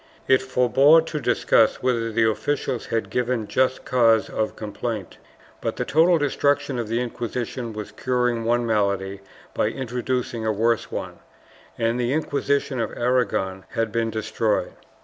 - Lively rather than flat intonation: No, narrow, 2.6 semitones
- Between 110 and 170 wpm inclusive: Yes, average, 150 wpm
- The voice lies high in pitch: No, low, 120 Hz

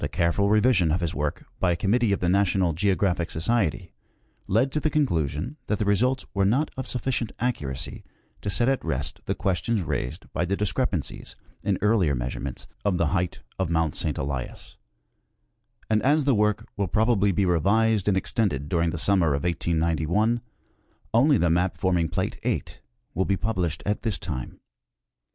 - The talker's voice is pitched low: Yes, very low, 95 Hz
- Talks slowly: No, average, 170 wpm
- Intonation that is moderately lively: Yes, average, 4.8 semitones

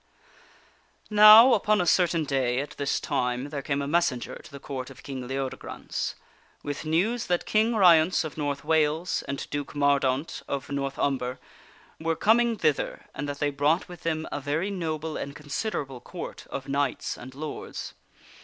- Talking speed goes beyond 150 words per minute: Yes, average, 170 wpm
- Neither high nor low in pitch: Yes, medium, 145 Hz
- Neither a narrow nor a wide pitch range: Yes, average, 3.6 semitones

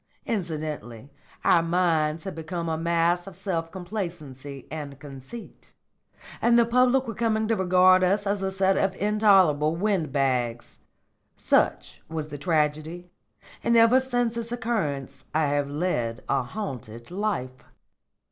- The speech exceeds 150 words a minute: No, average, 140 wpm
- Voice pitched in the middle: Yes, medium, 175 Hz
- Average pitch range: No, wide, 5.8 semitones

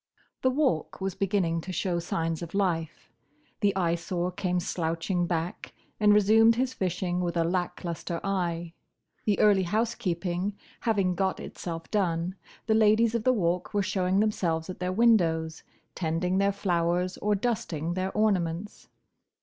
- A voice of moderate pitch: Yes, medium, 180 Hz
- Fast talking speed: No, average, 150 wpm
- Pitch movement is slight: No, average, 3.2 semitones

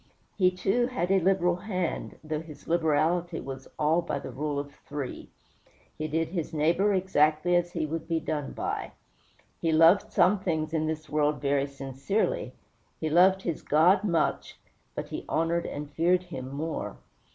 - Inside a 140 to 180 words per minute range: Yes, average, 170 wpm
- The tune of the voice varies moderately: Yes, average, 3.0 semitones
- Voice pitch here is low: No, medium, 165 Hz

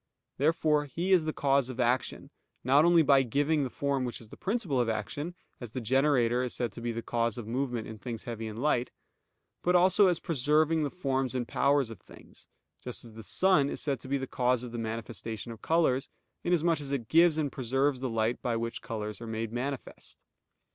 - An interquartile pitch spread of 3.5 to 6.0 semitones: Yes, average, 4.3 semitones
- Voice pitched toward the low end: Yes, low, 130 Hz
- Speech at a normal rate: No, fast, 215 wpm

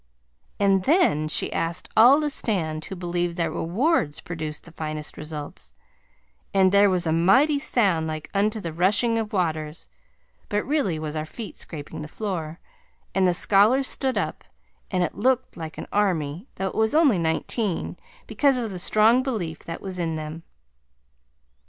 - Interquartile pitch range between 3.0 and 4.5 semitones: No, wide, 5.5 semitones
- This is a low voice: No, medium, 185 Hz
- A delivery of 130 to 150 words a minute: No, average, 165 wpm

